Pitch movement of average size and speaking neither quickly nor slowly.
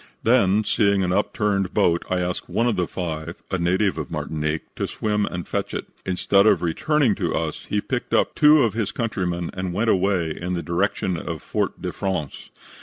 Yes: average, 3.4 semitones; average, 195 wpm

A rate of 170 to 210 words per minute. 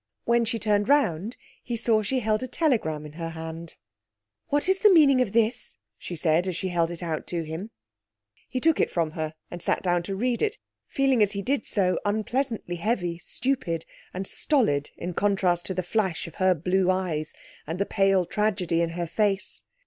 Yes: average, 195 wpm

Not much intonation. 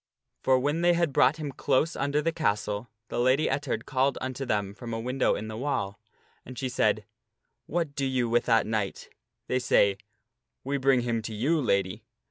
No: average, 4.0 semitones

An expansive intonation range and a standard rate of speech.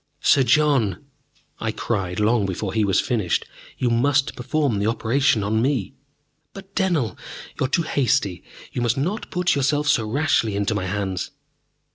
Yes: wide, 5.7 semitones; average, 160 wpm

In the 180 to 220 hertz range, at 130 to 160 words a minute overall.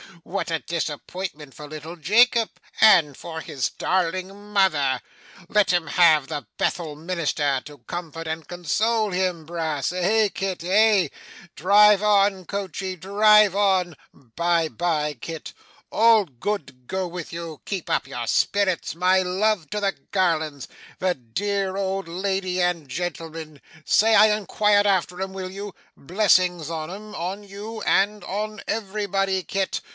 Yes: medium, 185 Hz; average, 140 wpm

